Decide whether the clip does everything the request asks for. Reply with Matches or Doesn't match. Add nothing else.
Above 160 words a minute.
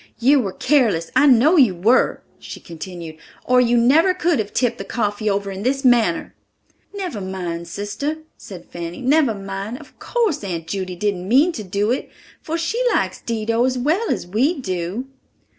Matches